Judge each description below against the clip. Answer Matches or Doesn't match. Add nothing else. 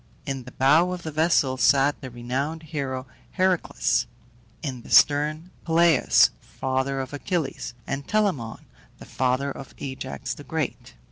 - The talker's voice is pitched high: Doesn't match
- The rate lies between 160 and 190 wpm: Doesn't match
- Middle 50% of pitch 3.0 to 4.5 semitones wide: Matches